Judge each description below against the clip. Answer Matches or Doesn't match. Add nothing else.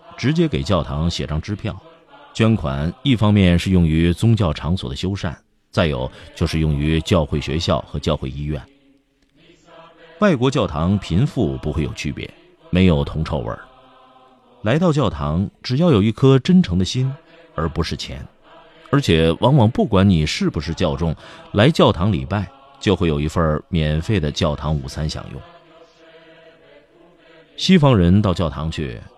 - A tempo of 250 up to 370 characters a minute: Doesn't match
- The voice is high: Doesn't match